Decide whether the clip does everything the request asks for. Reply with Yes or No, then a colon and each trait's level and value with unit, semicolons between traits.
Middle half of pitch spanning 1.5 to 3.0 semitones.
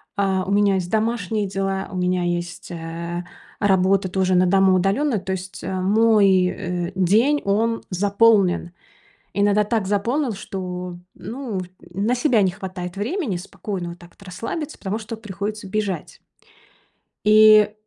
Yes: average, 2.7 semitones